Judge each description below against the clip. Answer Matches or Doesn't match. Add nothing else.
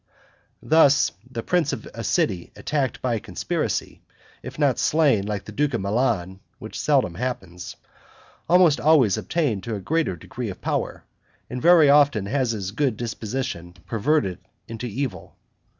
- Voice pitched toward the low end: Matches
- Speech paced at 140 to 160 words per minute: Matches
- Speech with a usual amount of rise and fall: Doesn't match